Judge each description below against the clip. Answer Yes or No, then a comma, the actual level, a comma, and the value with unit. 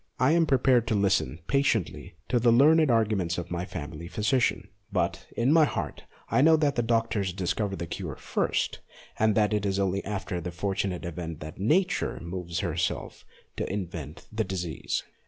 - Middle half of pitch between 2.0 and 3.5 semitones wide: No, wide, 5.4 semitones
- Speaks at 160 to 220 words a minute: Yes, average, 175 wpm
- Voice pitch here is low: Yes, low, 100 Hz